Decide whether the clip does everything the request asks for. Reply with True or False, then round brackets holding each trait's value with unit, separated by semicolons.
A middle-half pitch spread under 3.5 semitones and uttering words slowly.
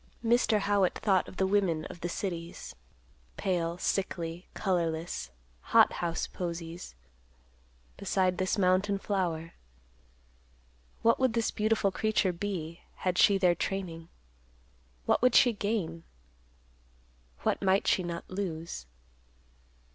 True (3.1 semitones; 115 wpm)